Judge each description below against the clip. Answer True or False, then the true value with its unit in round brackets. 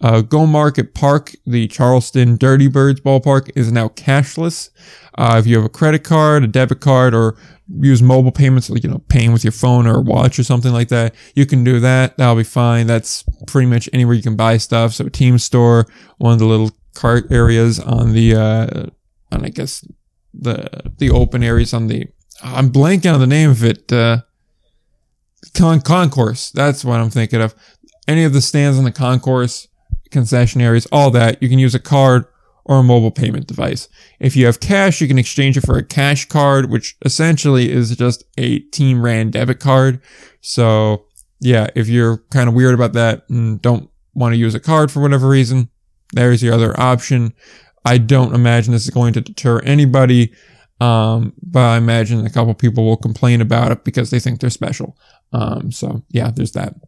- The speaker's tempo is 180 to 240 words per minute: True (195 wpm)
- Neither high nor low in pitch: False (125 Hz)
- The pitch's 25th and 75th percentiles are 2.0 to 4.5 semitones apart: True (2.7 semitones)